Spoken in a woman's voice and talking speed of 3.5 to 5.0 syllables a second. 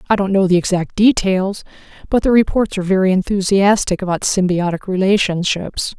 No: female; 5.5 syllables/s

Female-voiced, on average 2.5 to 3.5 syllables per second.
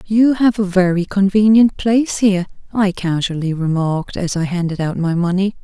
No: female; 5.2 syllables/s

